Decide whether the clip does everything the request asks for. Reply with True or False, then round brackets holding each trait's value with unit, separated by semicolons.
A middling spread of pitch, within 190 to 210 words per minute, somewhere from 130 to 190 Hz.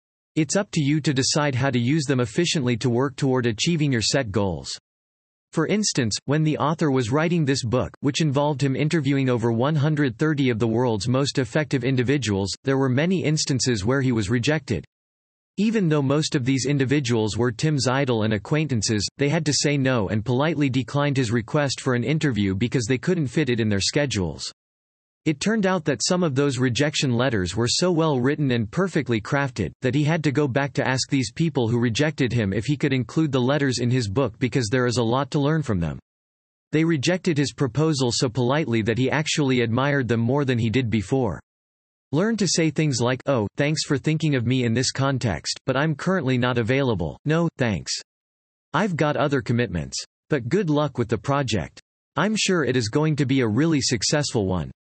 True (4.2 semitones; 200 wpm; 135 Hz)